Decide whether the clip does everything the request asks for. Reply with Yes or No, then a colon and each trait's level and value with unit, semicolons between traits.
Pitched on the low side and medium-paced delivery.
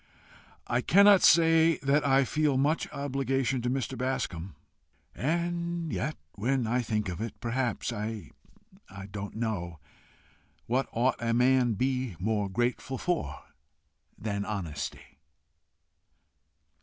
No: low, 125 Hz; slow, 120 wpm